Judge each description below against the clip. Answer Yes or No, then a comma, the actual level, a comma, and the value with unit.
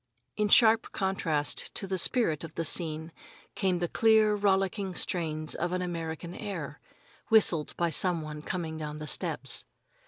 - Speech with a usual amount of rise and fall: Yes, average, 3.6 semitones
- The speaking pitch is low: No, medium, 175 Hz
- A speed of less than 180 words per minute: Yes, average, 155 wpm